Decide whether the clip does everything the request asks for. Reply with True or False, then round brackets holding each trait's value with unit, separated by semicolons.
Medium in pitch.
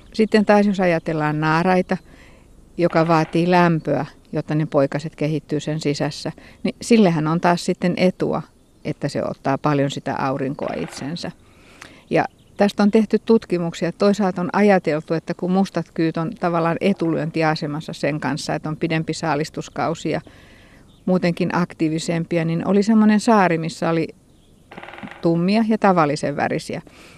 True (165 Hz)